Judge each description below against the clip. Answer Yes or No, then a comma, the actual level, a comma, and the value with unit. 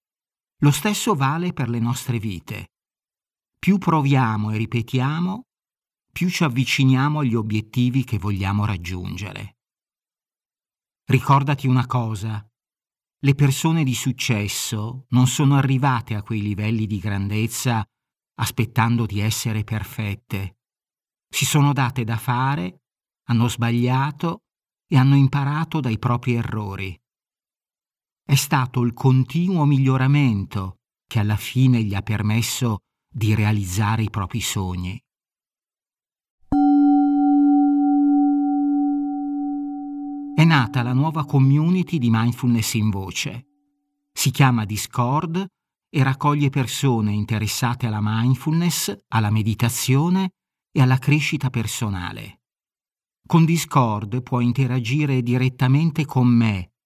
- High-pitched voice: No, low, 130 Hz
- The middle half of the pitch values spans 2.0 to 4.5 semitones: No, average, 5.0 semitones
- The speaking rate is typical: No, slow, 105 wpm